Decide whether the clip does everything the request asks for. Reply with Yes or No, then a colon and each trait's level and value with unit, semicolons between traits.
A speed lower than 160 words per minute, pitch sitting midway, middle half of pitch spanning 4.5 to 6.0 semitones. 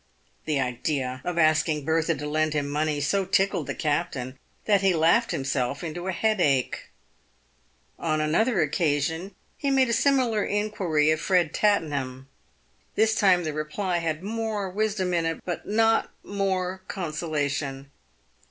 Yes: average, 150 wpm; medium, 165 Hz; average, 4.9 semitones